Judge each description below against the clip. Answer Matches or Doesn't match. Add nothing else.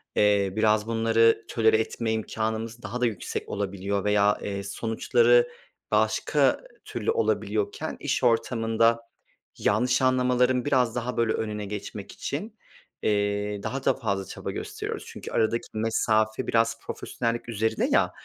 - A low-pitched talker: Matches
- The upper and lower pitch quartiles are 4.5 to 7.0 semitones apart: Doesn't match